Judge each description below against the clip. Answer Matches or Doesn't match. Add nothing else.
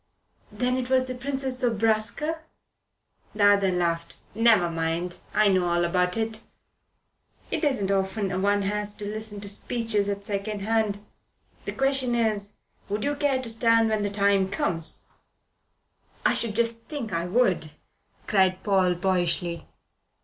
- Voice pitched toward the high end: Matches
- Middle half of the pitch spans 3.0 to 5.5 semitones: Matches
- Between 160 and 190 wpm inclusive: Doesn't match